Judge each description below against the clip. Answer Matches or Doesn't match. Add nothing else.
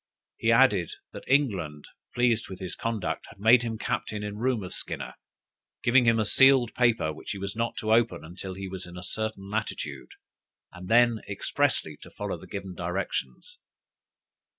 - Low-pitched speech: Matches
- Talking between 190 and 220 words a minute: Doesn't match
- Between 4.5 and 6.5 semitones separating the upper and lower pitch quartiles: Doesn't match